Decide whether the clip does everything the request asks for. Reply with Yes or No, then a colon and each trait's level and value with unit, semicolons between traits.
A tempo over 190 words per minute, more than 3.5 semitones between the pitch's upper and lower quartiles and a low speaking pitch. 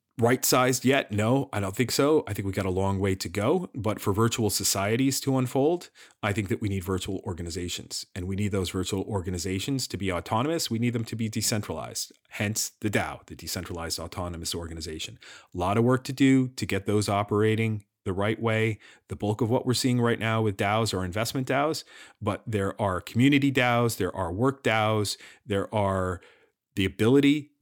Yes: average, 200 wpm; average, 4.1 semitones; low, 105 Hz